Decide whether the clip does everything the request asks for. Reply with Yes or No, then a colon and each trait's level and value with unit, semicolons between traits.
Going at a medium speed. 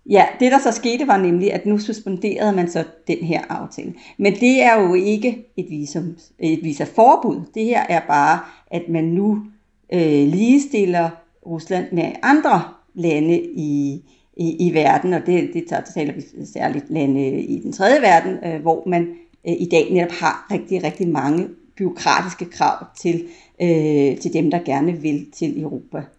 Yes: average, 175 wpm